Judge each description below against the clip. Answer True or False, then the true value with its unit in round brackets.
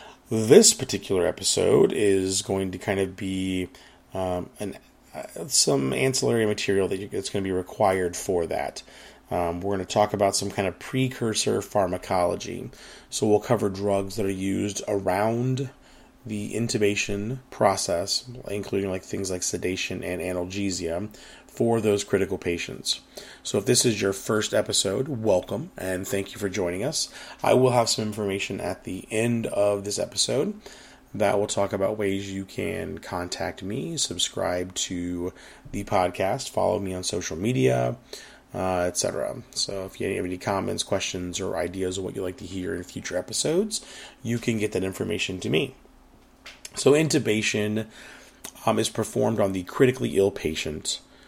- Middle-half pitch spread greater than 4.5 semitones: False (2.5 semitones)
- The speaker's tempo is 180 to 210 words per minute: False (160 wpm)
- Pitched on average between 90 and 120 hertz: True (100 Hz)